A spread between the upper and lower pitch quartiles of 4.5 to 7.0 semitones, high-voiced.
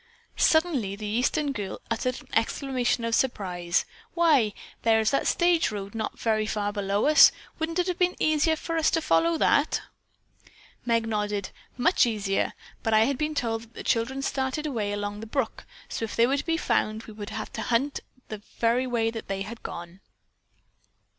Yes: average, 5.2 semitones; high, 230 Hz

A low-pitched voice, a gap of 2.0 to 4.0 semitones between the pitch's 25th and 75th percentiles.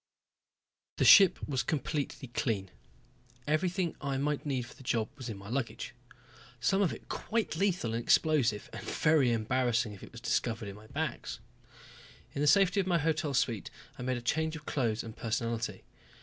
No: low, 130 Hz; average, 5.2 semitones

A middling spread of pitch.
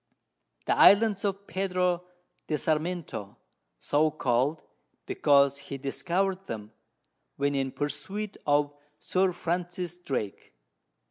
Yes: average, 4.6 semitones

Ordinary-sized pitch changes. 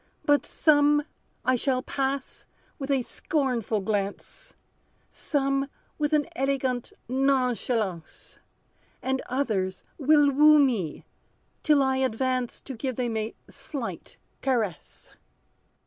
Yes: average, 3.3 semitones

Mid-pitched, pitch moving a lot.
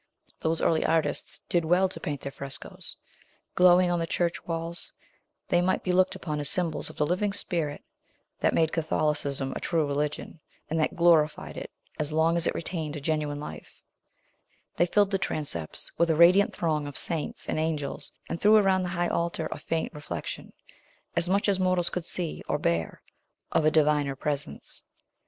No: medium, 165 Hz; average, 2.8 semitones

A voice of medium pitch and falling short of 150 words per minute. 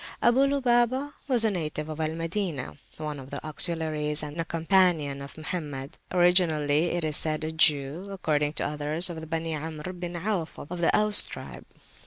No: medium, 160 Hz; average, 180 wpm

